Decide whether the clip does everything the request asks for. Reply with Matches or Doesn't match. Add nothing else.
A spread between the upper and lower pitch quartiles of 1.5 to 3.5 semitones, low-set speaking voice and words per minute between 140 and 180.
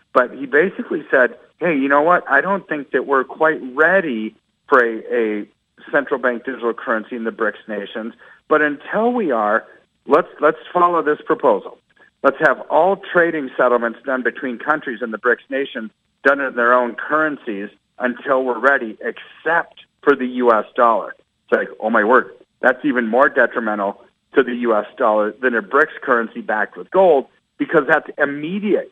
Doesn't match